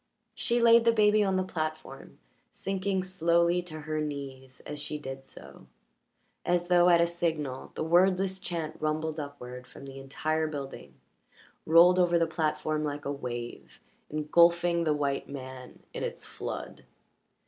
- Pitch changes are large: No, average, 3.6 semitones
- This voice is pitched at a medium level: Yes, medium, 155 Hz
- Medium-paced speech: Yes, average, 150 wpm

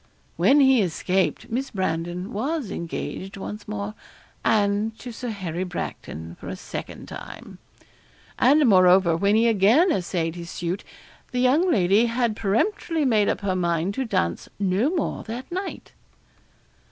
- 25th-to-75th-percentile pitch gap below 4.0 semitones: No, wide, 5.6 semitones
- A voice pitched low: No, high, 205 Hz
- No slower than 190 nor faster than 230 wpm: No, average, 145 wpm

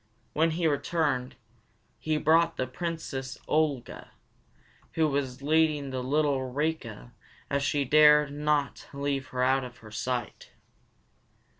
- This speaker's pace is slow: Yes, slow, 130 wpm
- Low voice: No, medium, 145 Hz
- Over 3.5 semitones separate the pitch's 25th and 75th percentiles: No, average, 3.0 semitones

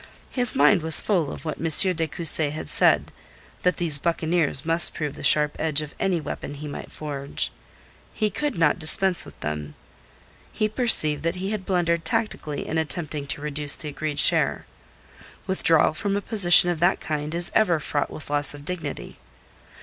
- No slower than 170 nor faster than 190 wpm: Yes, average, 180 wpm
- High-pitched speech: No, medium, 160 Hz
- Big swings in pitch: No, average, 3.4 semitones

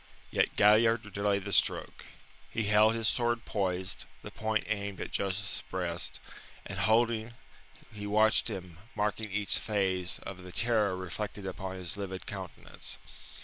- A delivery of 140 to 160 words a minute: Yes, average, 145 wpm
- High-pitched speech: No, low, 100 Hz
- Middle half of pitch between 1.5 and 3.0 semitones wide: Yes, average, 2.7 semitones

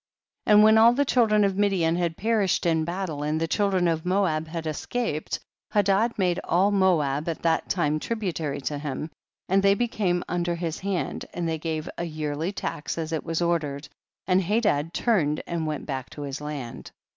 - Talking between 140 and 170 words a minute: No, average, 195 wpm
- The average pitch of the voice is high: No, medium, 170 Hz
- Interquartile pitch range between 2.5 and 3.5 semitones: No, average, 4.2 semitones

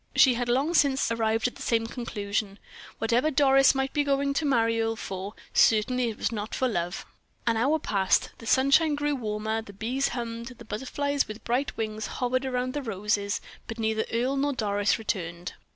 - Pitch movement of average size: Yes, average, 3.7 semitones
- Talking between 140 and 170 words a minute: No, average, 185 wpm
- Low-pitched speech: No, high, 235 Hz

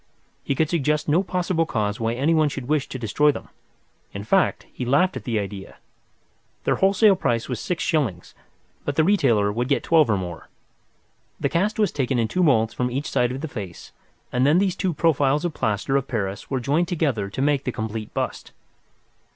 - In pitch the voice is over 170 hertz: No, low, 135 Hz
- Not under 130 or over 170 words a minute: No, average, 195 wpm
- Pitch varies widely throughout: Yes, wide, 6.2 semitones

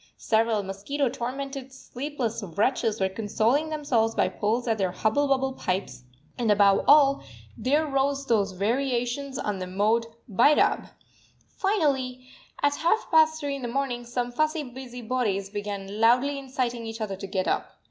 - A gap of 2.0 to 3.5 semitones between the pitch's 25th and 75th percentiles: No, average, 4.6 semitones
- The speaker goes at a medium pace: Yes, average, 155 wpm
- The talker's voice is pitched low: No, high, 245 Hz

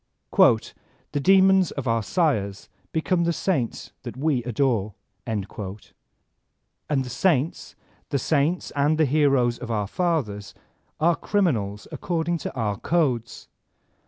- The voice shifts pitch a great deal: Yes, wide, 6.5 semitones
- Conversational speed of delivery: No, slow, 125 wpm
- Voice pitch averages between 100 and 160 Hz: Yes, medium, 140 Hz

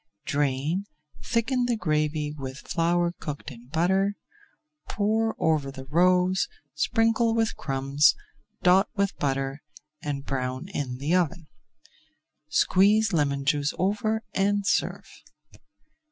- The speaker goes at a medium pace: No, slow, 110 wpm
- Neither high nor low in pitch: Yes, medium, 165 Hz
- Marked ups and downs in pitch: Yes, wide, 6.1 semitones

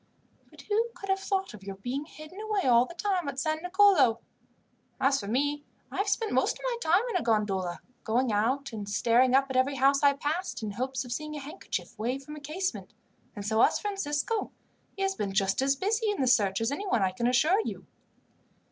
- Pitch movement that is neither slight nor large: No, wide, 8.1 semitones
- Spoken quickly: Yes, fast, 220 wpm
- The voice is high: Yes, very high, 275 Hz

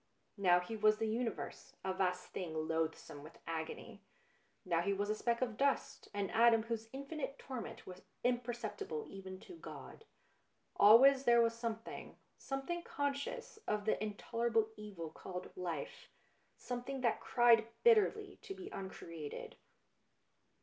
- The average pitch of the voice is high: Yes, high, 225 Hz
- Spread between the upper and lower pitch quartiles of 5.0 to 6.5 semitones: Yes, wide, 5.5 semitones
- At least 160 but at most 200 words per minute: No, average, 145 wpm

